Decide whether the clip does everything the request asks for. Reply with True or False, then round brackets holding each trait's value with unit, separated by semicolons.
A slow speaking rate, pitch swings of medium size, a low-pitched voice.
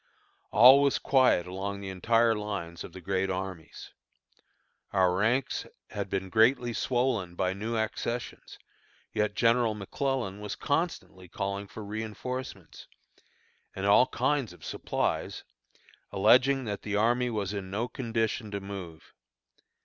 True (130 wpm; 3.8 semitones; 105 Hz)